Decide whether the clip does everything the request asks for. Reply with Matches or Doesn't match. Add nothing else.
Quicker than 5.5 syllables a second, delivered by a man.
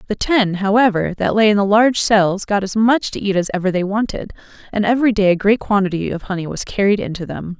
Doesn't match